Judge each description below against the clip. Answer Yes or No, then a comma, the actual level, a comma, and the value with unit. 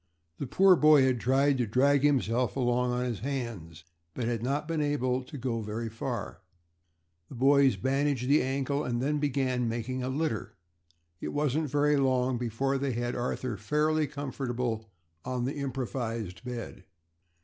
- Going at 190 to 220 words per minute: No, average, 160 wpm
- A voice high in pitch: No, low, 130 Hz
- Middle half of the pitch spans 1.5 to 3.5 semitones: Yes, average, 2.8 semitones